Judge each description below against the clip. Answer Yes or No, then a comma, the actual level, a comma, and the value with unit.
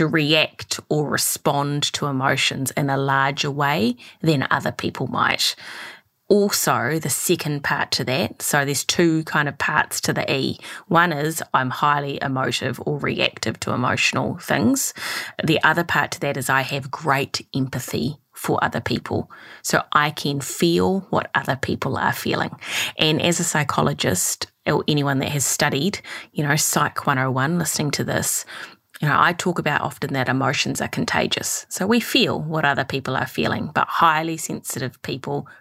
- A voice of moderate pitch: Yes, medium, 145 Hz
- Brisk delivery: No, average, 165 wpm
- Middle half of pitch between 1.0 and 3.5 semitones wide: Yes, average, 2.8 semitones